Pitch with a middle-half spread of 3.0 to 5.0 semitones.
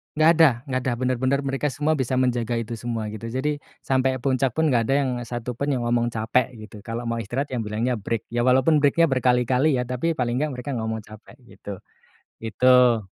No: narrow, 2.5 semitones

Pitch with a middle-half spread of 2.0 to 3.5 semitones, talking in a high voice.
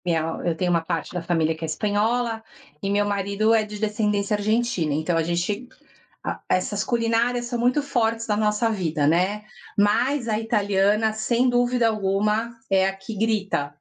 Yes: average, 3.2 semitones; high, 210 Hz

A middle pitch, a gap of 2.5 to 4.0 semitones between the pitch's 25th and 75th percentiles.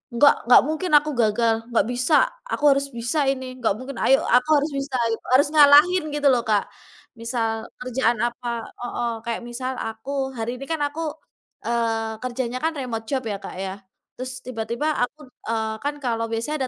No: very high, 250 Hz; average, 3.4 semitones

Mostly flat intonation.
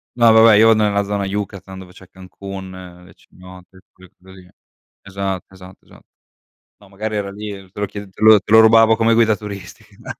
Yes: narrow, 2.3 semitones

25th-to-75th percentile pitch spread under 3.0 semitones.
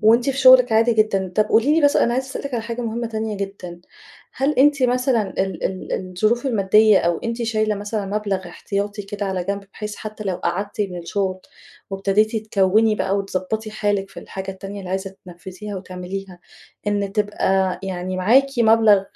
Yes: narrow, 2.6 semitones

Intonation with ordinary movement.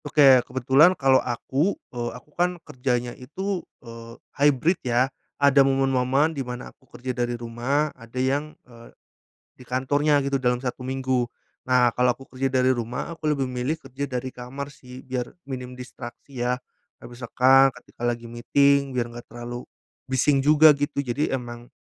No: narrow, 2.3 semitones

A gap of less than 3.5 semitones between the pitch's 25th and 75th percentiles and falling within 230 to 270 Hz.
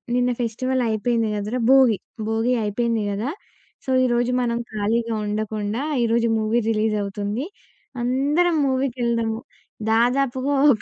Yes: narrow, 2.6 semitones; high, 235 Hz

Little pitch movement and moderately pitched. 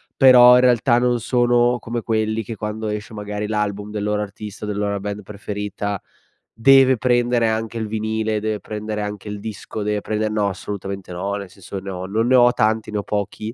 No: narrow, 1.8 semitones; low, 105 Hz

